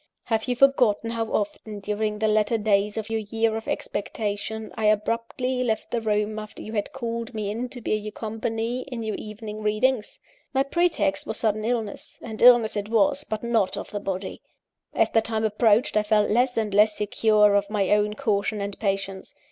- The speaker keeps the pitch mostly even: Yes, narrow, 1.7 semitones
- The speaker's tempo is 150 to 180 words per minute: No, average, 195 wpm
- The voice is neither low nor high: No, high, 220 Hz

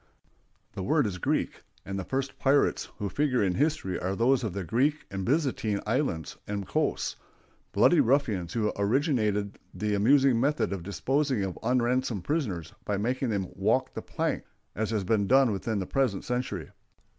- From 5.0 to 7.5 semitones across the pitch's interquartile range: Yes, average, 5.3 semitones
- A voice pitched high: No, low, 110 Hz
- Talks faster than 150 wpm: Yes, average, 165 wpm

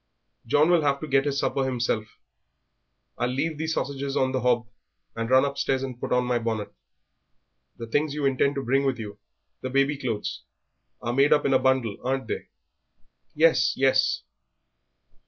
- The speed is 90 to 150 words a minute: No, average, 175 wpm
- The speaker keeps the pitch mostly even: Yes, narrow, 2.3 semitones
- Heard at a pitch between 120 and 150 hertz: Yes, low, 135 Hz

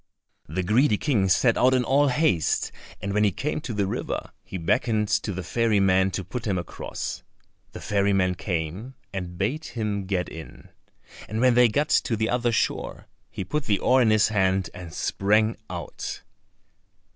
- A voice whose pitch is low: Yes, low, 105 Hz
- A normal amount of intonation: Yes, average, 4.2 semitones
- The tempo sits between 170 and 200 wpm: Yes, average, 180 wpm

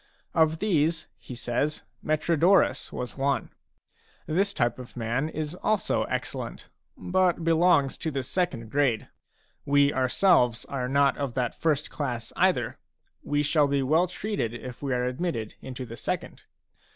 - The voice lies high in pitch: No, medium, 145 Hz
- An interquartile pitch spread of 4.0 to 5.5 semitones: Yes, average, 4.6 semitones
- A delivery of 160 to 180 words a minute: No, average, 145 wpm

